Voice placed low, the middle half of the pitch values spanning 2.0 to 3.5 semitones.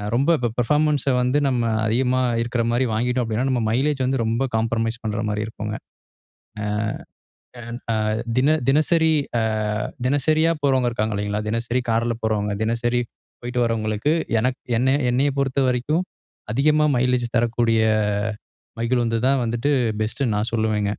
Yes: low, 120 Hz; average, 2.9 semitones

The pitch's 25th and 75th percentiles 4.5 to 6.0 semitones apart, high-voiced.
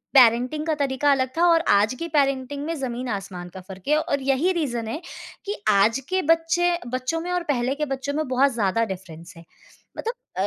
Yes: average, 5.2 semitones; very high, 270 Hz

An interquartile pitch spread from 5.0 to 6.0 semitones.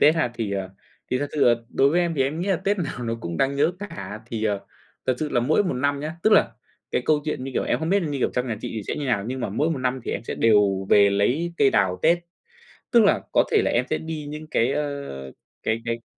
Yes: wide, 5.6 semitones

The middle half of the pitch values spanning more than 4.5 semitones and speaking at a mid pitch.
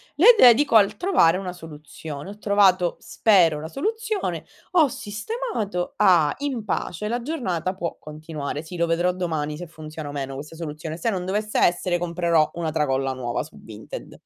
Yes: average, 5.3 semitones; medium, 175 Hz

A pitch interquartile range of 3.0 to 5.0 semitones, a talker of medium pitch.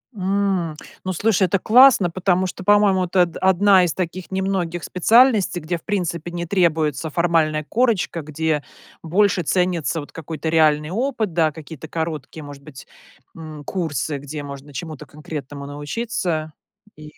Yes: average, 3.6 semitones; medium, 170 Hz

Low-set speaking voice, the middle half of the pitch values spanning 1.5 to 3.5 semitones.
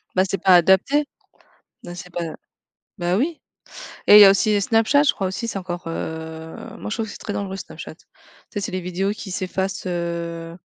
No: high, 190 Hz; average, 2.9 semitones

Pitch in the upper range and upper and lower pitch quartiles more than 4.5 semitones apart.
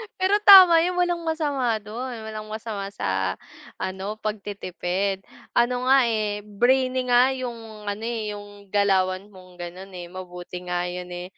Yes: high, 210 Hz; average, 5.0 semitones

